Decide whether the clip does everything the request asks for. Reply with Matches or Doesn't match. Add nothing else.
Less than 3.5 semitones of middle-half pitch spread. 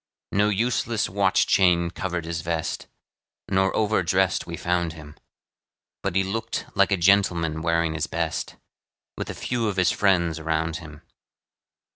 Matches